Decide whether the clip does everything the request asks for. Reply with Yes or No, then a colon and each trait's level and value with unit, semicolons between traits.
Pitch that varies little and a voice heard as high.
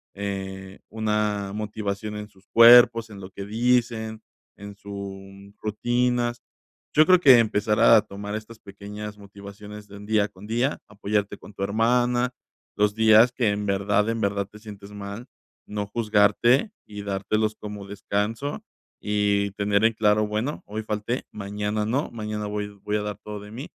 No: narrow, 1.7 semitones; low, 105 Hz